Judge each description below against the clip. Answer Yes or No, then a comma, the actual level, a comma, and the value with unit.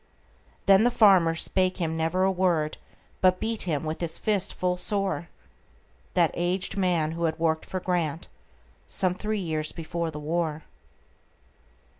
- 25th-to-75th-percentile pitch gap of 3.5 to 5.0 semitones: No, average, 2.8 semitones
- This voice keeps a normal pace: No, slow, 130 wpm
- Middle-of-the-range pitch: Yes, medium, 170 Hz